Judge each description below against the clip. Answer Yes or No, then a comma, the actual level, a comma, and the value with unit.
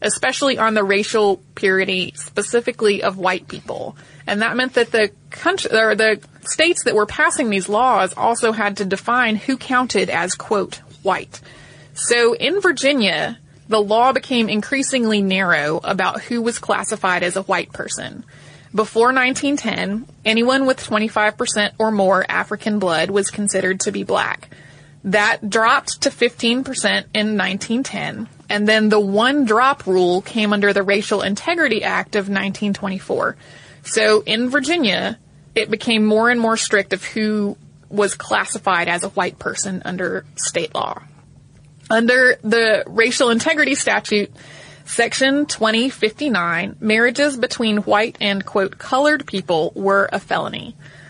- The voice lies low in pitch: No, high, 215 Hz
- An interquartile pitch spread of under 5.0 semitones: Yes, average, 3.6 semitones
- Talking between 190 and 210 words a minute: No, average, 140 wpm